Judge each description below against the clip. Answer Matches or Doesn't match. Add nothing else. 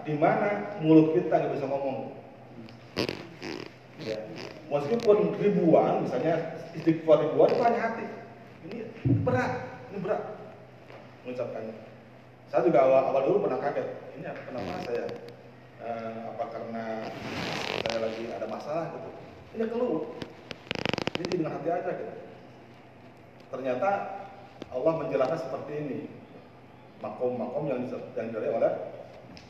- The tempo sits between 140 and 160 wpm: Doesn't match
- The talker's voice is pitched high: Doesn't match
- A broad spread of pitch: Matches